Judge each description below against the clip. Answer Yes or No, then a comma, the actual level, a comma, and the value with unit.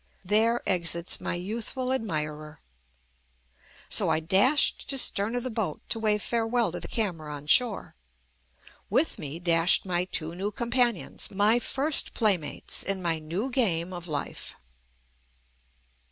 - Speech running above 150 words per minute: No, average, 140 wpm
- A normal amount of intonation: No, wide, 5.8 semitones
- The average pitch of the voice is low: No, high, 195 Hz